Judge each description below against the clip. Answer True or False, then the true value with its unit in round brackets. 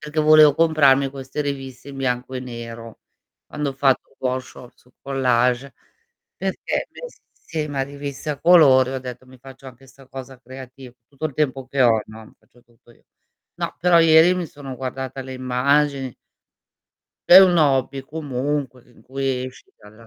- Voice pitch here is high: False (135 Hz)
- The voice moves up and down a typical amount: False (2.1 semitones)